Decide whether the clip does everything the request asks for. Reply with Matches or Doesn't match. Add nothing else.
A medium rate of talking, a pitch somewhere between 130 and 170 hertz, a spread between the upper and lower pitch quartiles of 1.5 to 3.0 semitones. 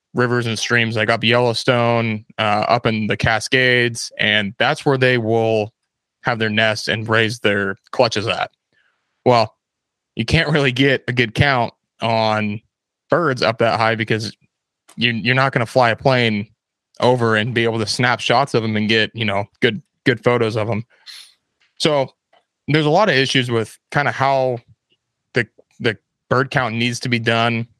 Doesn't match